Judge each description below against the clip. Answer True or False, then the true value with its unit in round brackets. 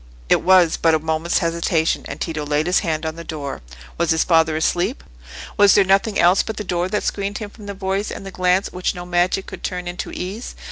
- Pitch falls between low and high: True (180 Hz)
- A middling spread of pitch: True (3.0 semitones)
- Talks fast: True (230 wpm)